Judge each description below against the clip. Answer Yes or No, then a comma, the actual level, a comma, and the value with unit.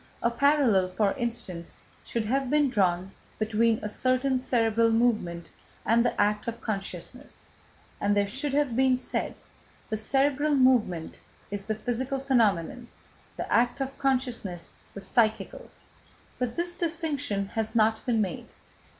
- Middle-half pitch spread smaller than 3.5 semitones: No, average, 4.1 semitones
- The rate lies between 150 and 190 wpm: No, average, 140 wpm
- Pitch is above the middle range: Yes, high, 235 Hz